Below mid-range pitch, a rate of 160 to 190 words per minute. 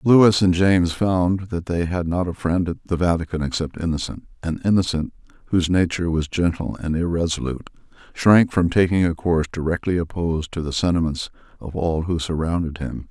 Yes: very low, 85 Hz; average, 175 wpm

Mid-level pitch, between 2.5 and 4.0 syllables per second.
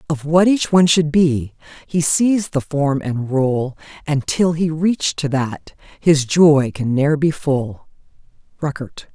Yes: medium, 150 Hz; 3.8 syllables/s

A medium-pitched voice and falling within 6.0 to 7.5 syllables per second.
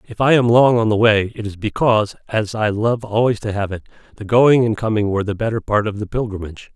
No: low, 110 Hz; 6.1 syllables/s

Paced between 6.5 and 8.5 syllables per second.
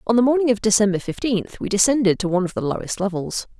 Yes: 6.8 syllables/s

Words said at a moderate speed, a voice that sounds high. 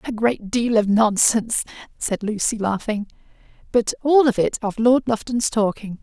Yes: average, 160 wpm; high, 220 Hz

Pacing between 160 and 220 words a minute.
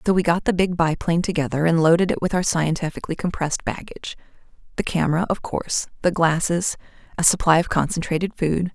Yes: average, 180 wpm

